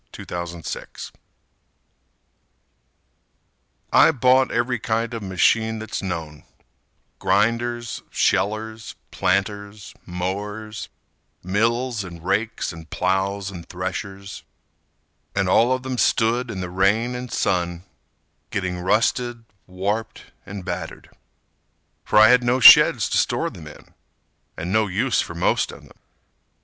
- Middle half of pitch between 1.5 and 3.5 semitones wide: No, average, 4.0 semitones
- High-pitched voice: No, low, 105 Hz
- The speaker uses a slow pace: Yes, slow, 115 wpm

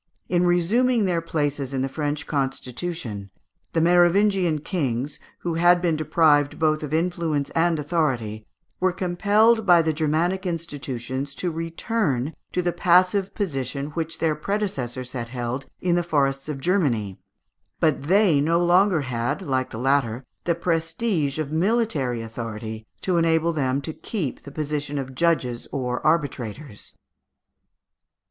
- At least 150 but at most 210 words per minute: No, average, 140 wpm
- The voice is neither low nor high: Yes, medium, 155 Hz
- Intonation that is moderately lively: Yes, average, 4.5 semitones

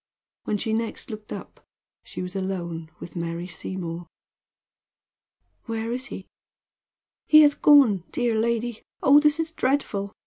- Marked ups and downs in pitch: Yes, wide, 5.9 semitones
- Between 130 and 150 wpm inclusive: Yes, slow, 135 wpm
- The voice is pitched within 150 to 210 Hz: No, high, 220 Hz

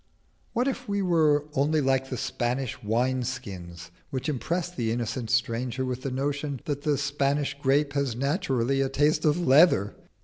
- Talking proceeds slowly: No, average, 165 wpm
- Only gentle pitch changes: No, average, 3.1 semitones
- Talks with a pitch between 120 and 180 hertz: Yes, low, 135 Hz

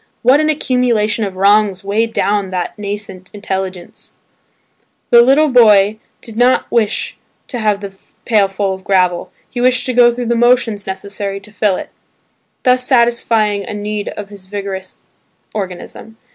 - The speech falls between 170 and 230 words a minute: No, average, 155 wpm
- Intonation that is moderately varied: Yes, average, 3.3 semitones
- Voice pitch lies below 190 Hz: No, high, 210 Hz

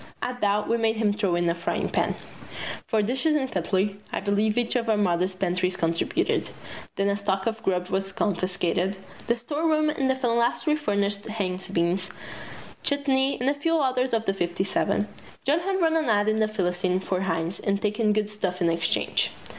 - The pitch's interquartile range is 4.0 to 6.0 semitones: Yes, average, 4.7 semitones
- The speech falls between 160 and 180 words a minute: No, average, 190 wpm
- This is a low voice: No, high, 205 Hz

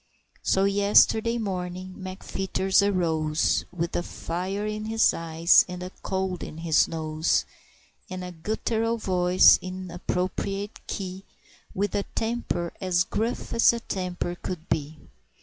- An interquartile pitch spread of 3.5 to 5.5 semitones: No, narrow, 2.6 semitones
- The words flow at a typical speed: No, slow, 130 wpm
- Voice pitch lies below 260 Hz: Yes, medium, 185 Hz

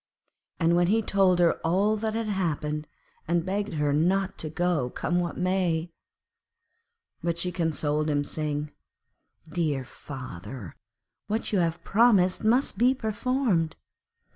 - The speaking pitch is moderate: Yes, medium, 175 Hz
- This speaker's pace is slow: Yes, slow, 130 wpm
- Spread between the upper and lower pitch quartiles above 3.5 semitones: Yes, average, 4.7 semitones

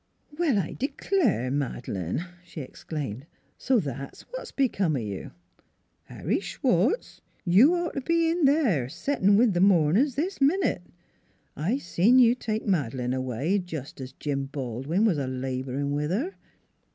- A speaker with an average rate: Yes, average, 150 wpm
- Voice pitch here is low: No, medium, 175 Hz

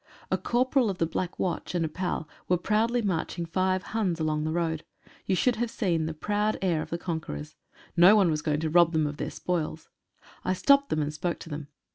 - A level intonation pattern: No, average, 4.0 semitones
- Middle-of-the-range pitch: Yes, medium, 175 Hz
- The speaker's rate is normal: No, fast, 220 wpm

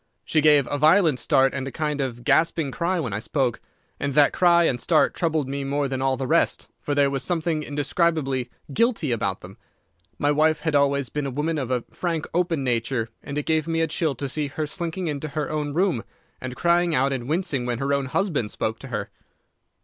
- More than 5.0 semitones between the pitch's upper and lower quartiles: No, average, 3.3 semitones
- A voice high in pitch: No, medium, 145 Hz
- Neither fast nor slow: No, fast, 220 wpm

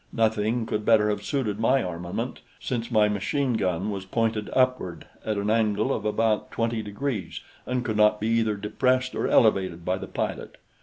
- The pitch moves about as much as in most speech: No, narrow, 2.1 semitones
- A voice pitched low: Yes, low, 110 Hz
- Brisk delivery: No, average, 175 wpm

